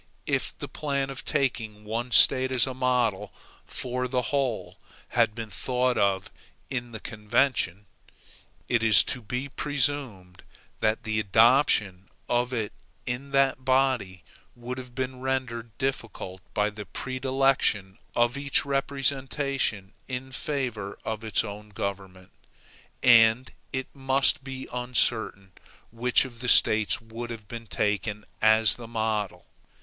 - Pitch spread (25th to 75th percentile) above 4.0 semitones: No, average, 3.6 semitones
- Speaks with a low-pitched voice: Yes, low, 120 Hz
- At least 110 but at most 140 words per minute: Yes, slow, 135 wpm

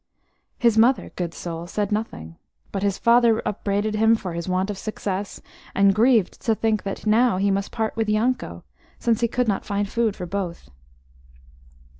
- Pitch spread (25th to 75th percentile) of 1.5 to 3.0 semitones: Yes, narrow, 2.6 semitones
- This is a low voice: No, high, 210 Hz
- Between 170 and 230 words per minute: Yes, average, 175 wpm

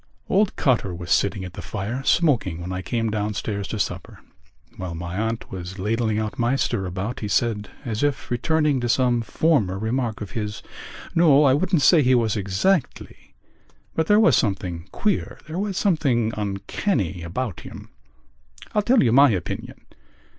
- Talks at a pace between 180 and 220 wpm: No, average, 165 wpm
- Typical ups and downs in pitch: No, wide, 6.3 semitones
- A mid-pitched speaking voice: No, low, 115 Hz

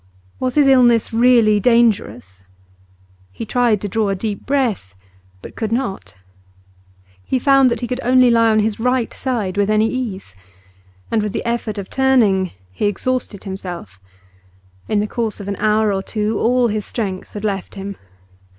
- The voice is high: Yes, high, 220 Hz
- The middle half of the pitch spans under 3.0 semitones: No, average, 3.5 semitones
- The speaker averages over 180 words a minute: No, average, 170 wpm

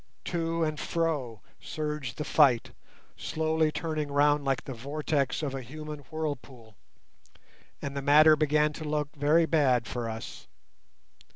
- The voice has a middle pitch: Yes, medium, 150 Hz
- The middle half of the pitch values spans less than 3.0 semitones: Yes, narrow, 2.4 semitones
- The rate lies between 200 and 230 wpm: No, slow, 135 wpm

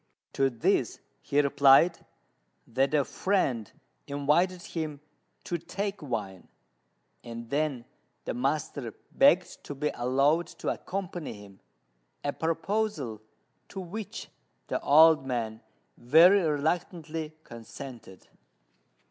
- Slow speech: Yes, slow, 105 wpm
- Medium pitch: Yes, medium, 145 Hz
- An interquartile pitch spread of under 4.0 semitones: No, average, 5.3 semitones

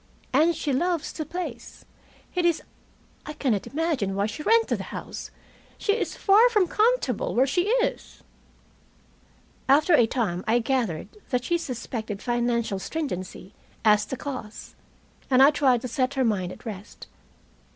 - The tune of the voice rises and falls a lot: Yes, wide, 6.9 semitones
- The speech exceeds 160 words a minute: No, average, 150 wpm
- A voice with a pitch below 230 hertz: No, very high, 260 Hz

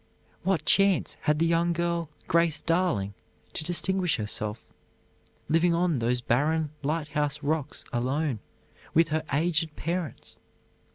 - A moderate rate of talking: No, slow, 120 wpm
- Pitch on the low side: No, medium, 160 Hz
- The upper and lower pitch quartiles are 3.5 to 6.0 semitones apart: No, average, 3.0 semitones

